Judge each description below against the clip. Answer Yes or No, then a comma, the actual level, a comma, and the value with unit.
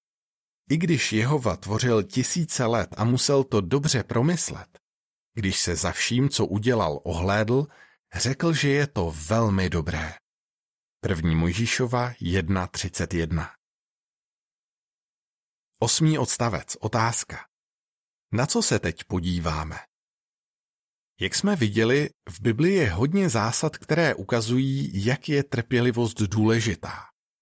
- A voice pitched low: Yes, low, 115 Hz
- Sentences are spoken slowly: Yes, slow, 110 wpm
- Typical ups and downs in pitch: No, wide, 5.9 semitones